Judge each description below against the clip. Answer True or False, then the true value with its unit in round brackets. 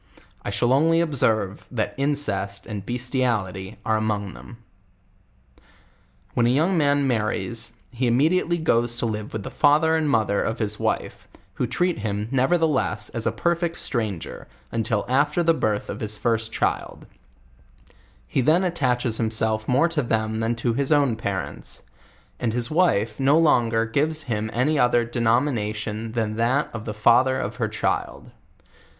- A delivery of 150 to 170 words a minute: True (155 wpm)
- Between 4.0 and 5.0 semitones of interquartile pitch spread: True (4.7 semitones)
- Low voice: True (120 Hz)